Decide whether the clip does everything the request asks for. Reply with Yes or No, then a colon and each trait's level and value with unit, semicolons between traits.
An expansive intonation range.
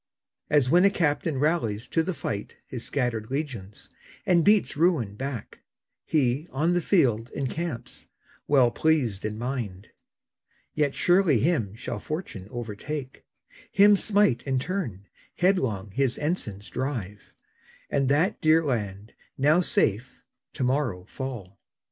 Yes: wide, 6.3 semitones